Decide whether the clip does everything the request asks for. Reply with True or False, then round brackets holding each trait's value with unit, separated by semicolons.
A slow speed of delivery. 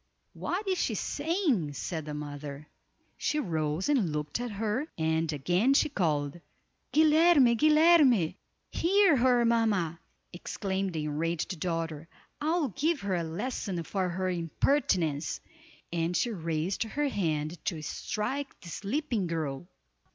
True (130 wpm)